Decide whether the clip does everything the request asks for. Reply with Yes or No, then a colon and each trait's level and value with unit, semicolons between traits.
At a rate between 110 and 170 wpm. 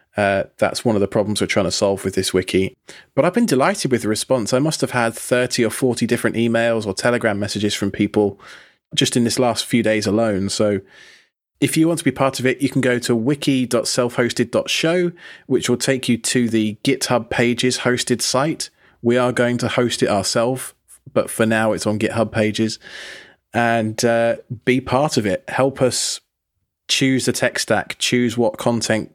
No: average, 195 wpm